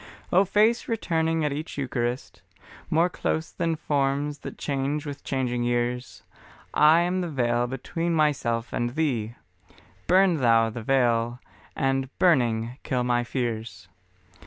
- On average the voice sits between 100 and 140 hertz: Yes, low, 135 Hz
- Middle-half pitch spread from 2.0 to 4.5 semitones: No, average, 4.9 semitones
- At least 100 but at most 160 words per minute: Yes, slow, 135 wpm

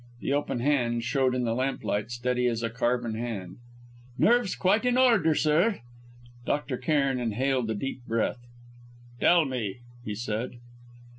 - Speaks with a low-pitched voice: Yes, low, 125 Hz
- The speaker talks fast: No, average, 145 wpm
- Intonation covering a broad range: No, average, 4.0 semitones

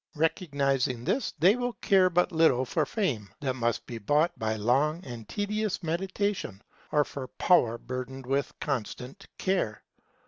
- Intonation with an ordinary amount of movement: No, wide, 6.8 semitones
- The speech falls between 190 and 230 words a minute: No, average, 145 wpm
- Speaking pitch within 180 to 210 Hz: No, medium, 140 Hz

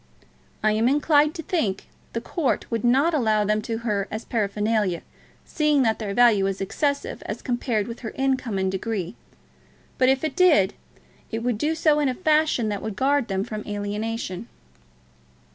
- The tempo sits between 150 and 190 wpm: Yes, average, 175 wpm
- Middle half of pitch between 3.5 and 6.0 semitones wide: Yes, average, 5.0 semitones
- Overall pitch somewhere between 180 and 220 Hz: No, high, 230 Hz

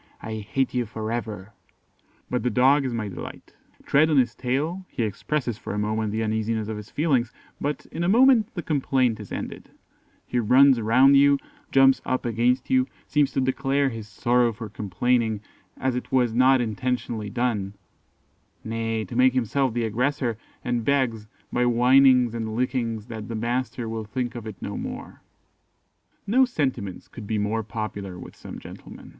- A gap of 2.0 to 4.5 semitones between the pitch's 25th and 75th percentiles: Yes, average, 3.2 semitones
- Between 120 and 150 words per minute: No, average, 175 wpm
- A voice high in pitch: No, low, 120 Hz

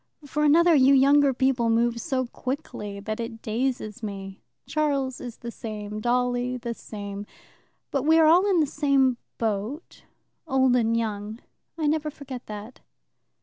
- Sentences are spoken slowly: No, average, 150 wpm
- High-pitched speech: Yes, very high, 250 Hz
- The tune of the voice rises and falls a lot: No, average, 4.2 semitones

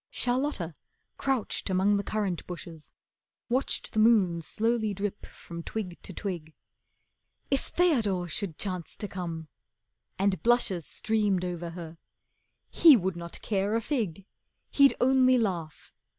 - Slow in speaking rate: Yes, slow, 130 wpm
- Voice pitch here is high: Yes, high, 195 Hz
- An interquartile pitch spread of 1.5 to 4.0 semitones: No, average, 4.7 semitones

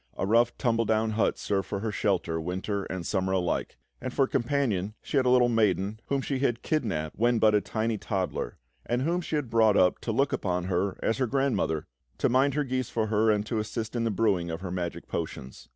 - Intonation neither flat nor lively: Yes, average, 4.3 semitones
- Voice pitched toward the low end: Yes, low, 110 Hz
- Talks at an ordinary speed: No, fast, 225 wpm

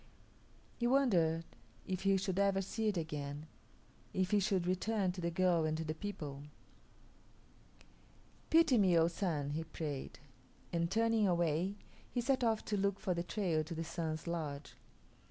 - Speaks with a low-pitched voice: No, medium, 180 Hz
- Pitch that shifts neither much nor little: Yes, average, 3.9 semitones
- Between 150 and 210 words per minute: Yes, average, 160 wpm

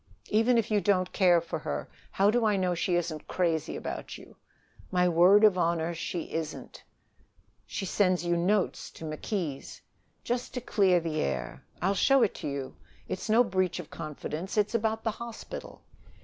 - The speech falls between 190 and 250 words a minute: No, average, 175 wpm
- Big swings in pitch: No, average, 4.0 semitones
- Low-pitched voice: No, medium, 185 Hz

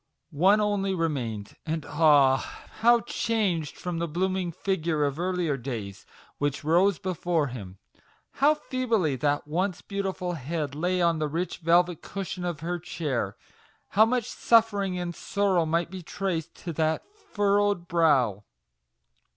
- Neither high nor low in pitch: Yes, medium, 170 Hz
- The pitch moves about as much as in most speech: Yes, average, 4.3 semitones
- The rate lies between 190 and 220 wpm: No, average, 140 wpm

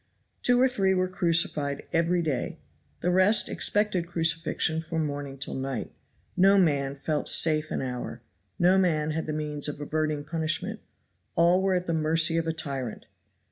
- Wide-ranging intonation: No, average, 3.2 semitones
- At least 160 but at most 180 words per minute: Yes, average, 165 wpm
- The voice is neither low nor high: Yes, medium, 160 Hz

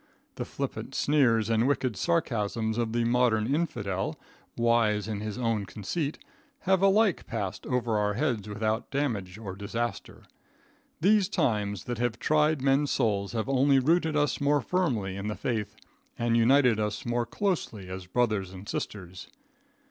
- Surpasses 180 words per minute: No, average, 150 wpm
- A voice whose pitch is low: Yes, low, 115 Hz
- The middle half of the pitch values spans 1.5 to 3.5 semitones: No, average, 4.9 semitones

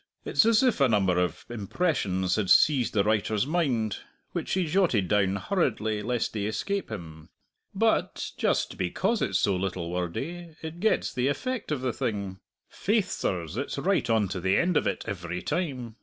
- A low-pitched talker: Yes, low, 110 Hz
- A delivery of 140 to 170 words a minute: No, average, 180 wpm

